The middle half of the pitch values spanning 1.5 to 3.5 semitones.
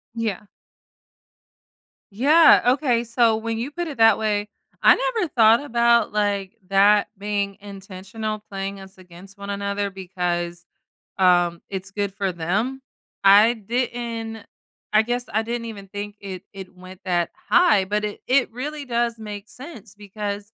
Yes: average, 3.1 semitones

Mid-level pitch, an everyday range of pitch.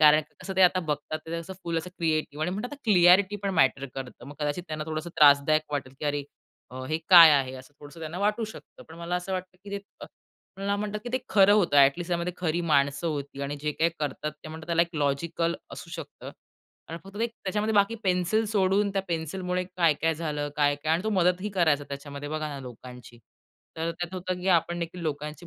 Yes: medium, 165 Hz; average, 3.9 semitones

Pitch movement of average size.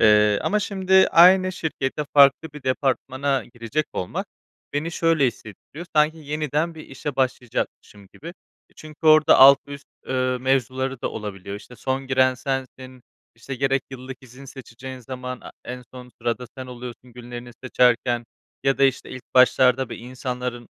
No: narrow, 2.3 semitones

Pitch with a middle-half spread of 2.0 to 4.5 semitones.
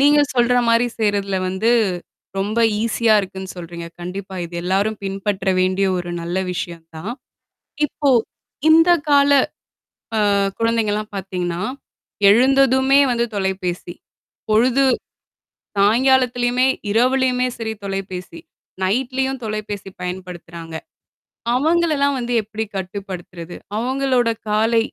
No: average, 5.0 semitones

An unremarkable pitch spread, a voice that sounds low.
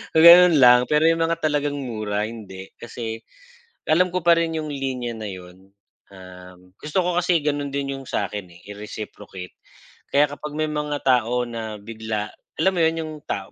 No: wide, 6.7 semitones; low, 130 Hz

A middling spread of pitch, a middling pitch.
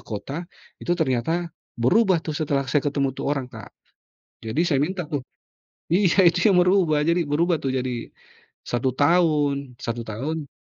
Yes: average, 4.5 semitones; medium, 150 Hz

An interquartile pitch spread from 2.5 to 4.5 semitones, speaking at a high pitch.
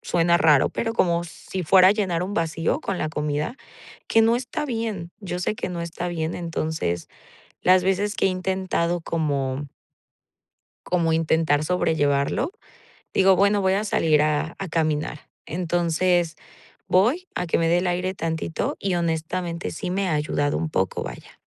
No: average, 2.9 semitones; medium, 170 Hz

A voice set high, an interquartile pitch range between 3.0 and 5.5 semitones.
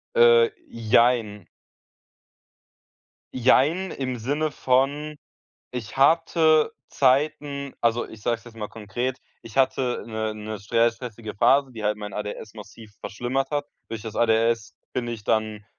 No: low, 120 Hz; average, 4.0 semitones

